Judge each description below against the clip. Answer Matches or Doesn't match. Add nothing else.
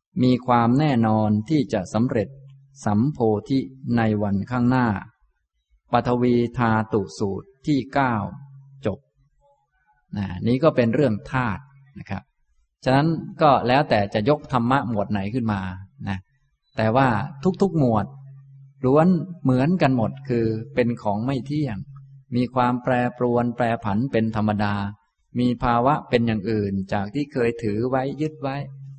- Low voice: Matches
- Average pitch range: Matches